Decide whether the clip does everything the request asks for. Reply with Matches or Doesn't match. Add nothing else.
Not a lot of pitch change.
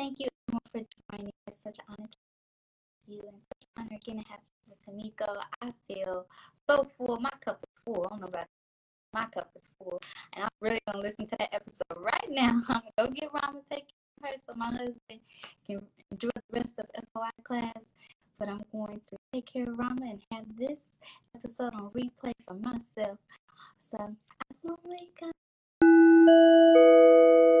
Doesn't match